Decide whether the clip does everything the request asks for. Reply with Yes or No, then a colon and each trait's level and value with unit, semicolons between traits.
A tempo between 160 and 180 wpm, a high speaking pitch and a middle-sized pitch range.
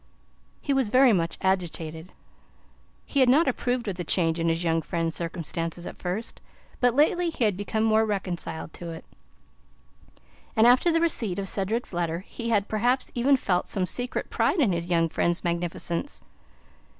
No: average, 170 wpm; high, 195 Hz; wide, 6.3 semitones